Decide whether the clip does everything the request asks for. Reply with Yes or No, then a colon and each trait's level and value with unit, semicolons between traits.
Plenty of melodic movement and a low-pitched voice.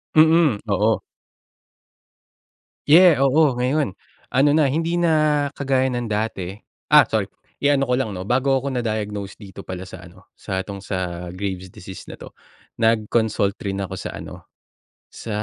Yes: wide, 6.3 semitones; low, 115 Hz